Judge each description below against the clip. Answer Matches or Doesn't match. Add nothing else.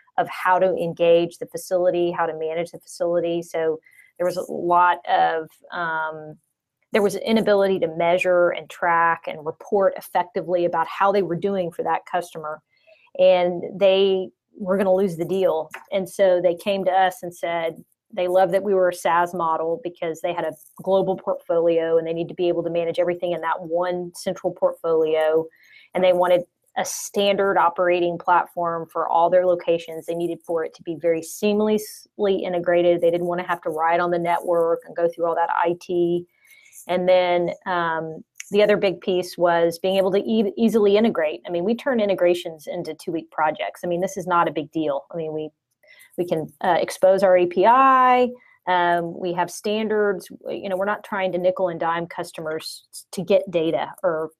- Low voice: Doesn't match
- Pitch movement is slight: Matches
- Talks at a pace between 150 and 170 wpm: Doesn't match